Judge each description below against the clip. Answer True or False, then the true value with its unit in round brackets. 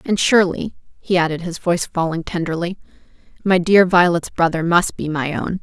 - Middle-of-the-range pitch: True (175 Hz)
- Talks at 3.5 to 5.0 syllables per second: False (5.4 syllables/s)